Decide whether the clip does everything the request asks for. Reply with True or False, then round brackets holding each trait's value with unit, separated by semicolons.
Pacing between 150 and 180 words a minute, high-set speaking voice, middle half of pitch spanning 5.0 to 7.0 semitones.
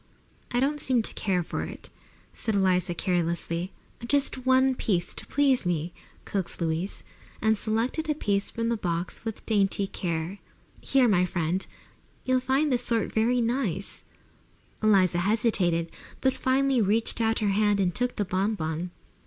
True (155 wpm; 210 Hz; 5.5 semitones)